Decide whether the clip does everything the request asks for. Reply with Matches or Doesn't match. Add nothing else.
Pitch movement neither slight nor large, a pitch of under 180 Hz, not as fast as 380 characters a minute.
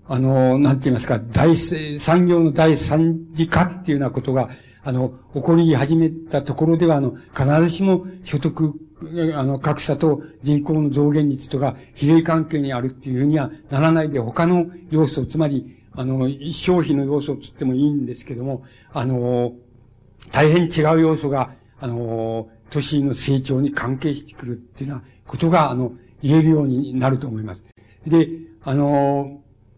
Matches